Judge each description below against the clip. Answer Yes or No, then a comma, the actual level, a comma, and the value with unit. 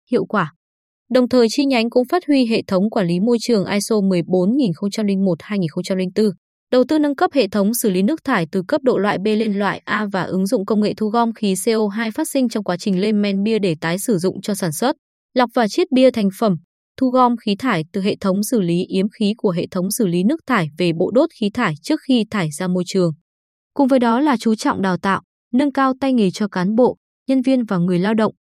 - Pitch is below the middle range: No, high, 215 Hz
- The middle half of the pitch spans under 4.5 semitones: No, average, 4.8 semitones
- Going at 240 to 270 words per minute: Yes, average, 245 wpm